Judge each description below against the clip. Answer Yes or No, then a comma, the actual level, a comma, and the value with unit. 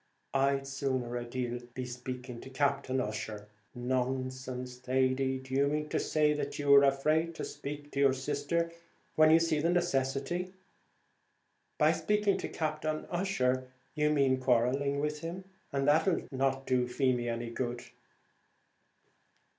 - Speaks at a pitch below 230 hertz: Yes, low, 135 Hz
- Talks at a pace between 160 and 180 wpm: No, average, 145 wpm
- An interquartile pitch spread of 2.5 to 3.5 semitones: Yes, average, 2.8 semitones